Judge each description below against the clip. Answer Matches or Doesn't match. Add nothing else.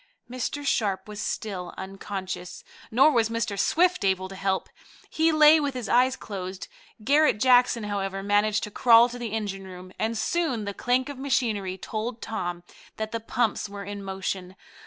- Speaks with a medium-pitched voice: Doesn't match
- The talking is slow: Doesn't match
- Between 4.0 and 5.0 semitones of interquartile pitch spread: Matches